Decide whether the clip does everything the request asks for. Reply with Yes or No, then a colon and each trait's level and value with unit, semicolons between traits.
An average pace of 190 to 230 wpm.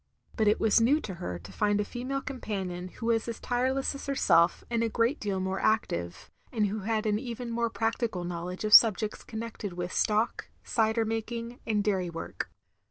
Yes: average, 195 wpm